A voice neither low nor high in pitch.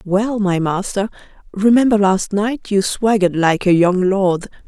No: high, 195 Hz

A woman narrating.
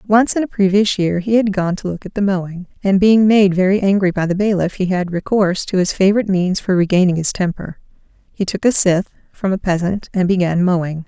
Yes: female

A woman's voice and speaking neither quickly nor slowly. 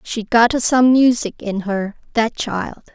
Yes: female; average, 165 wpm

